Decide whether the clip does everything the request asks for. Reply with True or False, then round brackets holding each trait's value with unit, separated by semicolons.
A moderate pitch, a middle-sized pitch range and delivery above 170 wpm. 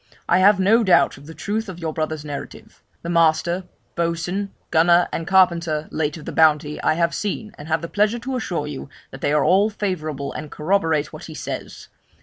True (170 Hz; 3.7 semitones; 200 wpm)